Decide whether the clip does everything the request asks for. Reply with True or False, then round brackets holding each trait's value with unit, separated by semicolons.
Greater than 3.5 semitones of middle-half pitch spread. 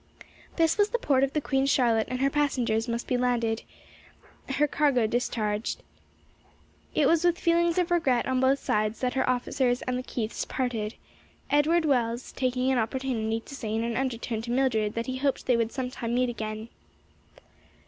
False (3.0 semitones)